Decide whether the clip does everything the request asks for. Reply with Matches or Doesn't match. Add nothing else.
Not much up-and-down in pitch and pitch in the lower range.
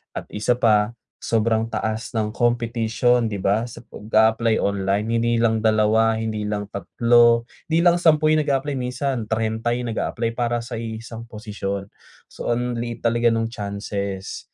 Matches